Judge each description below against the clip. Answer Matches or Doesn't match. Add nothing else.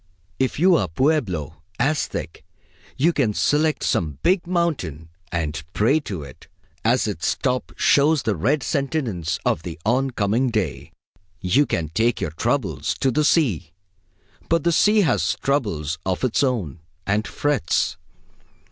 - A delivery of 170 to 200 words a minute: Doesn't match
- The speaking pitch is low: Matches